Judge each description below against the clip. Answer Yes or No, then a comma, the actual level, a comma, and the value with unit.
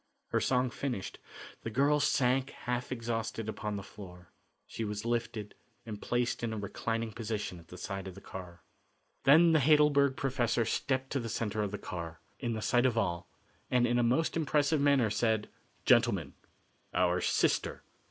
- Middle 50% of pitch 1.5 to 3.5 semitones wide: No, average, 4.0 semitones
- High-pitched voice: No, low, 115 Hz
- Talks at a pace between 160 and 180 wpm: Yes, average, 170 wpm